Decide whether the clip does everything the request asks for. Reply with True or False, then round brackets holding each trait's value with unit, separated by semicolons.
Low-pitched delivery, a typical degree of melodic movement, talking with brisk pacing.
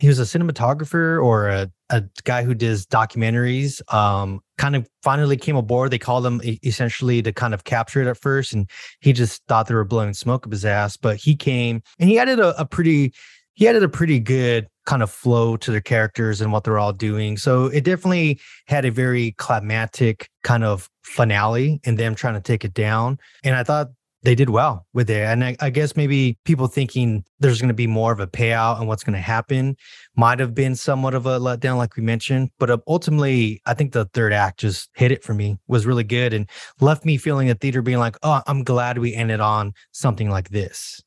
True (120 Hz; 3.6 semitones; 220 wpm)